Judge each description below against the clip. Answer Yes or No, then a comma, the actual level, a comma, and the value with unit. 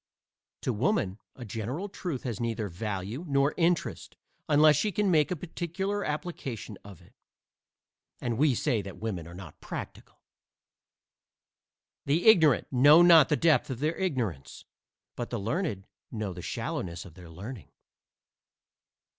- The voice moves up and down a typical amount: No, wide, 8.0 semitones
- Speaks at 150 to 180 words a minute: No, average, 140 wpm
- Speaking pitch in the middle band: No, low, 130 Hz